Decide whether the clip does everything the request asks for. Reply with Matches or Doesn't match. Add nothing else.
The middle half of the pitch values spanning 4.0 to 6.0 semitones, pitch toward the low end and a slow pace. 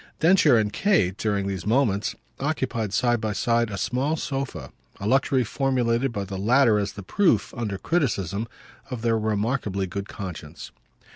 Doesn't match